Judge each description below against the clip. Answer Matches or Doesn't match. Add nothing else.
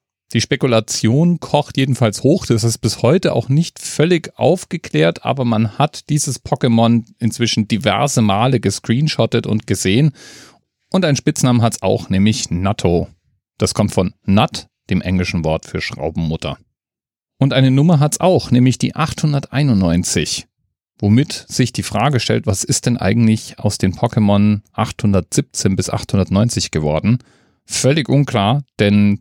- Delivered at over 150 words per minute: Doesn't match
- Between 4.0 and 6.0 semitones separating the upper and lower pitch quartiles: Matches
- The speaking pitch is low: Matches